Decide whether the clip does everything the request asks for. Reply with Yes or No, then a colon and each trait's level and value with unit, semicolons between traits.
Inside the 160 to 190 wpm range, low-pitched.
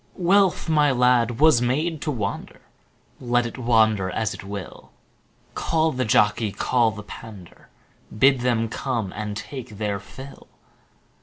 No: average, 140 wpm; low, 120 Hz